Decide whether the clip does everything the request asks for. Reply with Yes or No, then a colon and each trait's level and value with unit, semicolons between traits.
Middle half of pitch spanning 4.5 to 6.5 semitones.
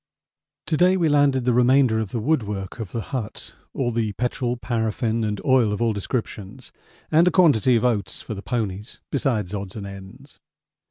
No: average, 3.8 semitones